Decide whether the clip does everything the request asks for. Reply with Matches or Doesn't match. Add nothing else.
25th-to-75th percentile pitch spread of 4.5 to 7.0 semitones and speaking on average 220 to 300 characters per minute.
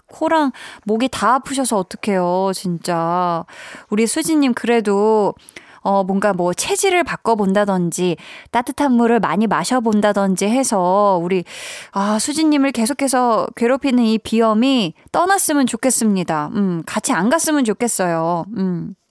Matches